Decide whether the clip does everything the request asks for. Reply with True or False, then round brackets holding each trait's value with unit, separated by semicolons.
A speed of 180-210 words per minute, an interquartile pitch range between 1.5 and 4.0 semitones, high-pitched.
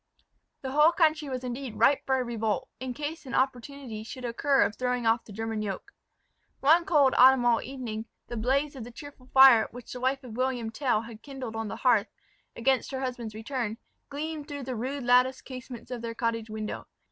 True (195 wpm; 2.9 semitones; 255 Hz)